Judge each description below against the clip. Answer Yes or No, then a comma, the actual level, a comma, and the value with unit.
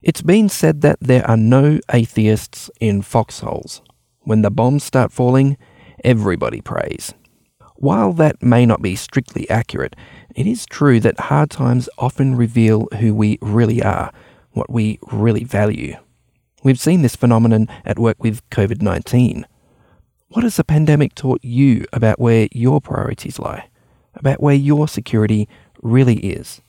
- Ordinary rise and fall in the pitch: Yes, average, 3.8 semitones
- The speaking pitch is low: Yes, low, 120 Hz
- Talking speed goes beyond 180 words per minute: No, average, 145 wpm